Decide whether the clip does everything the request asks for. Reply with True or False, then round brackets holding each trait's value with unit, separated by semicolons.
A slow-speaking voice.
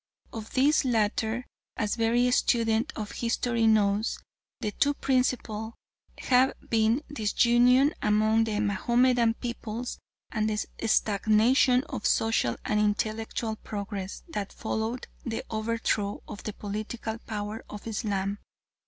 True (120 wpm)